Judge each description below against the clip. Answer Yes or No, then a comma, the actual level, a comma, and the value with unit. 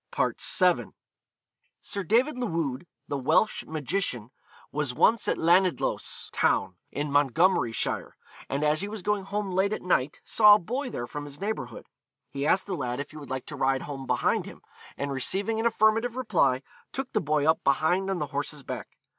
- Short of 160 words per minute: No, average, 180 wpm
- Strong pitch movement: Yes, wide, 6.6 semitones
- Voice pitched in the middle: Yes, medium, 160 Hz